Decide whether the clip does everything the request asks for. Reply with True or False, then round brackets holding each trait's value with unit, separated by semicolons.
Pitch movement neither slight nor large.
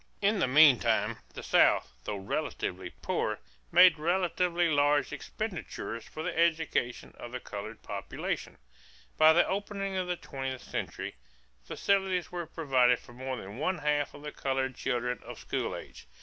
False (5.8 semitones)